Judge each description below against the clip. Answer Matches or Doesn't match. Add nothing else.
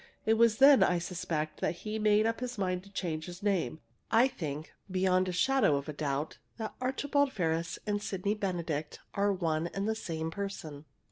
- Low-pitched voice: Doesn't match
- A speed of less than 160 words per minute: Doesn't match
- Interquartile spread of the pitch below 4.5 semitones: Doesn't match